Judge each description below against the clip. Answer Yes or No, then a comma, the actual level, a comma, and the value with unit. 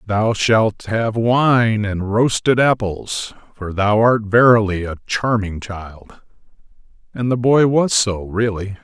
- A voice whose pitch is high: No, low, 110 Hz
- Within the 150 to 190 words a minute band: No, slow, 135 wpm